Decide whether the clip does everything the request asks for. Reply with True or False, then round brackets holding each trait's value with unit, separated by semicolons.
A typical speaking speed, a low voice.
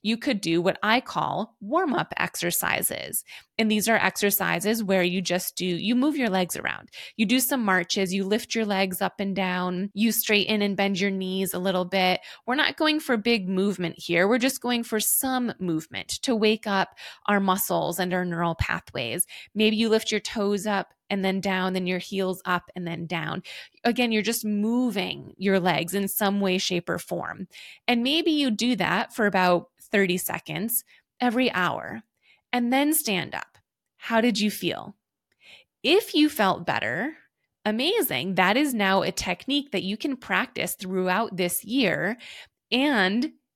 False (180 wpm; 200 Hz)